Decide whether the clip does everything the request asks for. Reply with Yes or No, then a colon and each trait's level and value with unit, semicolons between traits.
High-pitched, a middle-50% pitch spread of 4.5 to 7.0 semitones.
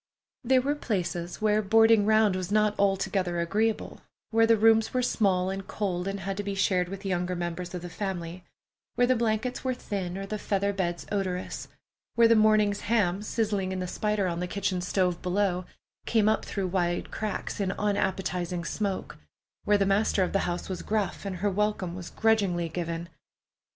No: high, 195 Hz; average, 2.9 semitones